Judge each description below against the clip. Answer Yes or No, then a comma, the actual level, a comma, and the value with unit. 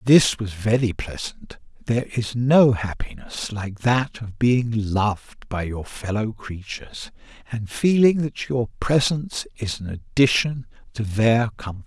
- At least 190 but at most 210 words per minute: No, average, 140 wpm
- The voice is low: Yes, low, 115 Hz